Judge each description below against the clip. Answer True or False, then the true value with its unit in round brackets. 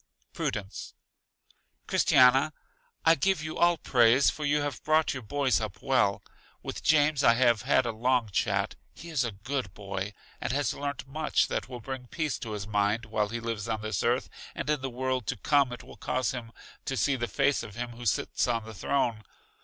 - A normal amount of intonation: True (4.1 semitones)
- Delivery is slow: False (200 wpm)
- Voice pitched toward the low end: True (125 Hz)